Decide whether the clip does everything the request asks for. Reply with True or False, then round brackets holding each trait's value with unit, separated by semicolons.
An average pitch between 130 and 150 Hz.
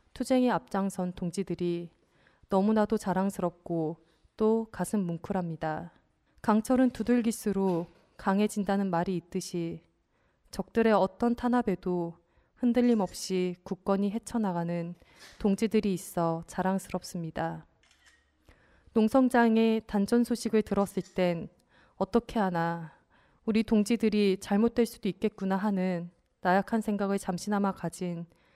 False (195 Hz)